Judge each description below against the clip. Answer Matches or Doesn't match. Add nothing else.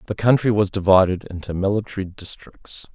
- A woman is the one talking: Doesn't match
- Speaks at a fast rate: Doesn't match